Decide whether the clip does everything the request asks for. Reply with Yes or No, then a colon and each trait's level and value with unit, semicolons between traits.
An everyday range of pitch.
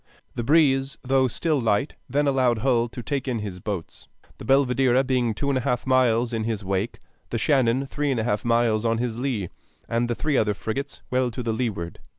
Yes: average, 3.0 semitones